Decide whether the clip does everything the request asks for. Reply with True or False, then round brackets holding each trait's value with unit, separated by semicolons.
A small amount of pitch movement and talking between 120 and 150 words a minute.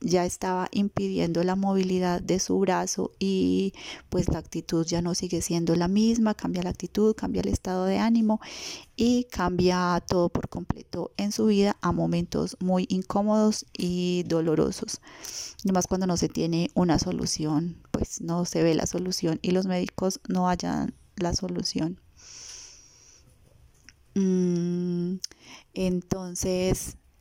True (2.1 semitones; 135 wpm)